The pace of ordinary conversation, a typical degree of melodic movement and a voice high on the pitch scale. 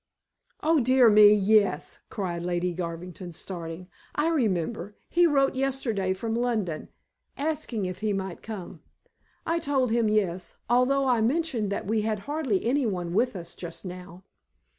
No: average, 145 wpm; wide, 6.0 semitones; high, 210 Hz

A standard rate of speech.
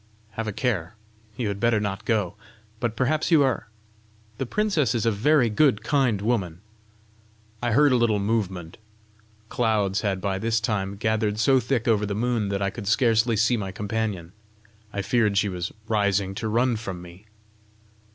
Yes: average, 170 wpm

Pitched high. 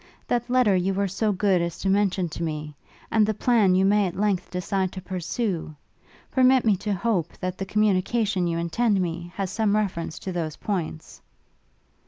Yes: high, 195 Hz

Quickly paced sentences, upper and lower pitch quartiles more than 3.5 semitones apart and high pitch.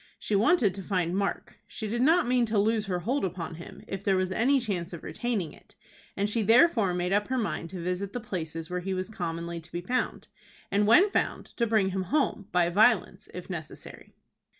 Yes: fast, 215 wpm; average, 4.2 semitones; high, 195 Hz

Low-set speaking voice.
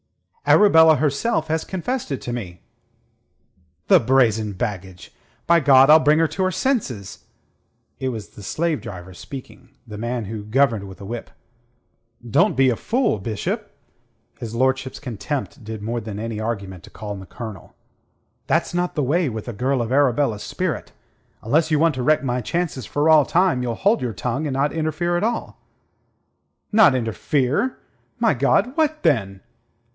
Yes: low, 130 Hz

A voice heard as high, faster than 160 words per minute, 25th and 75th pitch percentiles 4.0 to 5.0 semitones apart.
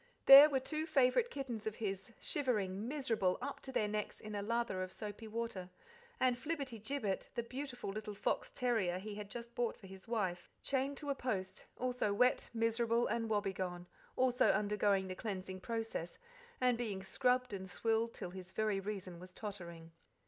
Yes: high, 220 Hz; average, 175 wpm; average, 4.4 semitones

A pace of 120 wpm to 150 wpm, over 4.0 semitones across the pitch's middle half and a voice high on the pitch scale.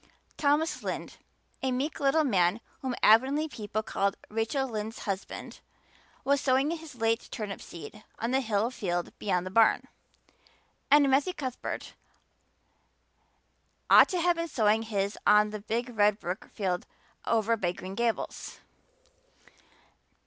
Yes: slow, 135 wpm; average, 4.6 semitones; high, 225 Hz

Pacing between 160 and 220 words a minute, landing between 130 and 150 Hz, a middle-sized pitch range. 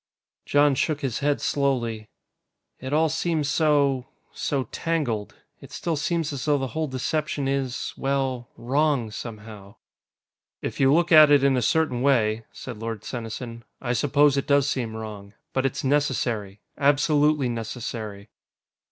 No: average, 145 wpm; low, 135 Hz; average, 4.0 semitones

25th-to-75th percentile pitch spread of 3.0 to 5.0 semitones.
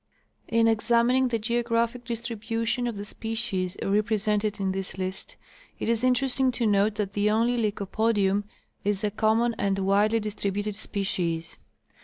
No: narrow, 2.5 semitones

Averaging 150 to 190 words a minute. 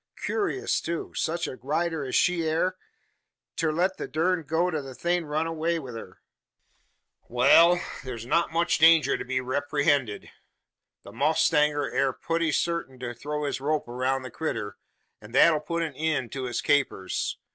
Yes: average, 170 wpm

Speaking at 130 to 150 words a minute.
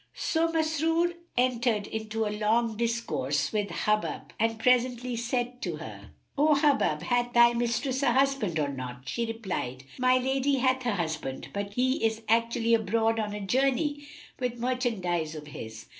No: average, 160 wpm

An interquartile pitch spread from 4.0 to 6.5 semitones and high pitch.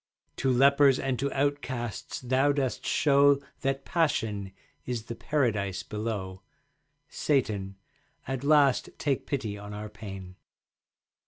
No: average, 5.0 semitones; low, 125 Hz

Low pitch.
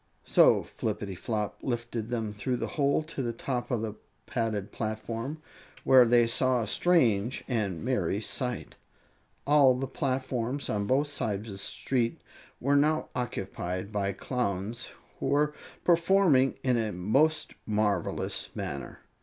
Yes: low, 120 Hz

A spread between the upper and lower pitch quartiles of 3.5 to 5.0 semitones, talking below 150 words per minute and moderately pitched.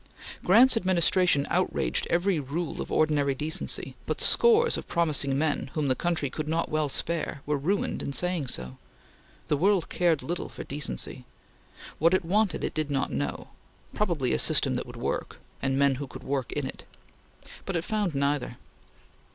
No: average, 4.2 semitones; average, 165 wpm; medium, 155 Hz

